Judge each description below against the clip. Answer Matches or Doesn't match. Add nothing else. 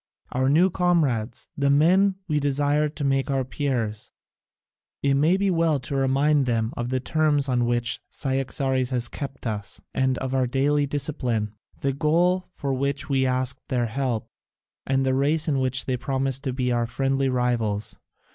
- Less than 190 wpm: Matches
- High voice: Doesn't match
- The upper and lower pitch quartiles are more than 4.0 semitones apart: Doesn't match